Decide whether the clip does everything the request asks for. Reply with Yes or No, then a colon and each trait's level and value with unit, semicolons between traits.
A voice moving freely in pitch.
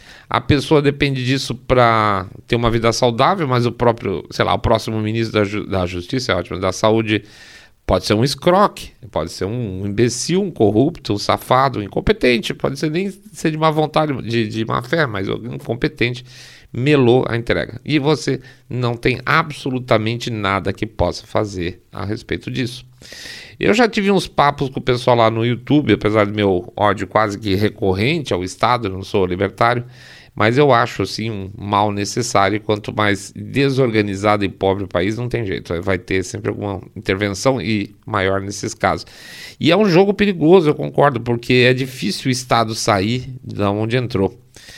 No: average, 4.0 semitones